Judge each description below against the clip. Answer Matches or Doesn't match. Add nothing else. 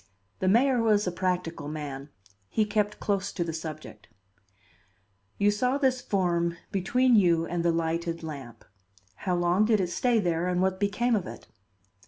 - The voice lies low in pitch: Doesn't match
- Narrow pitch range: Doesn't match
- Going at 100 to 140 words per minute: Doesn't match